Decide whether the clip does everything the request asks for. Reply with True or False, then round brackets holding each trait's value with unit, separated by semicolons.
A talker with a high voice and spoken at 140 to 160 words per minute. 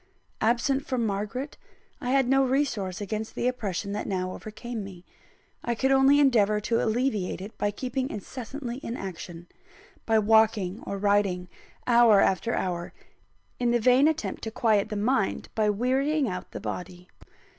True (220 Hz; 155 wpm)